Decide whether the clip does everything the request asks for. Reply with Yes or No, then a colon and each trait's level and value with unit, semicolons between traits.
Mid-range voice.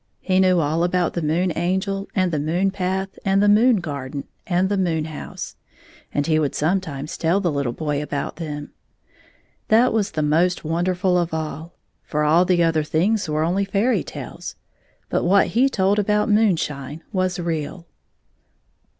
Yes: medium, 175 Hz